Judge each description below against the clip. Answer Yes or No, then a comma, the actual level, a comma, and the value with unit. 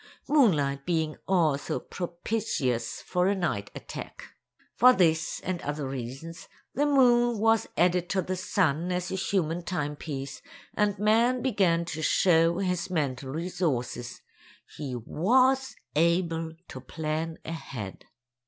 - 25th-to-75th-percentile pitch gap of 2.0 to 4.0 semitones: No, average, 4.5 semitones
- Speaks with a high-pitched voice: No, medium, 170 Hz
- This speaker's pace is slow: Yes, slow, 120 wpm